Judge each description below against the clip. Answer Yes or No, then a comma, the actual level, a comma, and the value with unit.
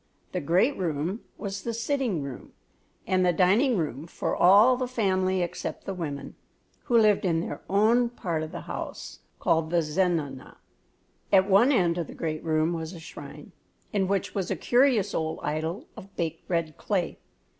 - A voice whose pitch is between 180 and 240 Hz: Yes, medium, 185 Hz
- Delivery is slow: No, average, 170 wpm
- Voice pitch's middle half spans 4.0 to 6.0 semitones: Yes, average, 4.4 semitones